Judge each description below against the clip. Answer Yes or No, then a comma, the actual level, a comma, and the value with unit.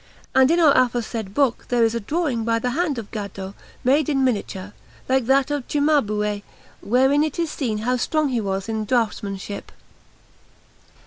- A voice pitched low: No, high, 245 Hz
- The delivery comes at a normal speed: Yes, average, 170 wpm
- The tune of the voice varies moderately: Yes, average, 4.9 semitones